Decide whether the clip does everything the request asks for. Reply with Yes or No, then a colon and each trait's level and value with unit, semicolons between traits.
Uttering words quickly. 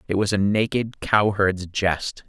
No: average, 185 wpm